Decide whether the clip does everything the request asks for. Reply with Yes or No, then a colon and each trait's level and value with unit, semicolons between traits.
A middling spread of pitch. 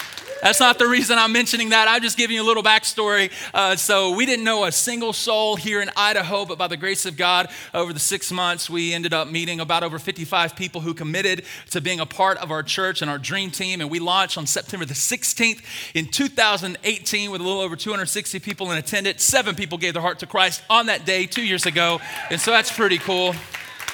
Yes: average, 3.6 semitones